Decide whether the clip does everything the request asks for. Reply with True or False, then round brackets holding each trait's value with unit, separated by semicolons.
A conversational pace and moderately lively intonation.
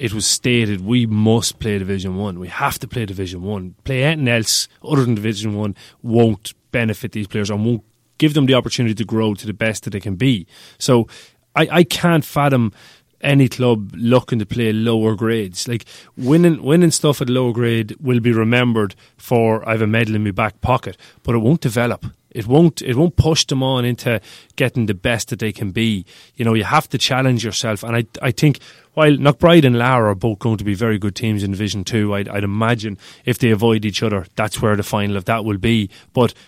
False (220 wpm; 3.0 semitones)